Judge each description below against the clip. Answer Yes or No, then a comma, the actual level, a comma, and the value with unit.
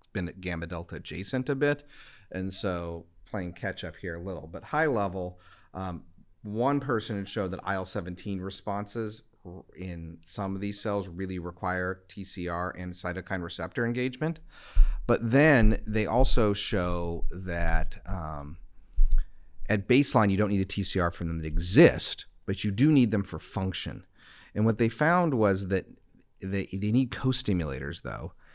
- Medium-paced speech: Yes, average, 155 wpm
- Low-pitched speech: Yes, very low, 95 Hz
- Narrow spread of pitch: No, average, 3.6 semitones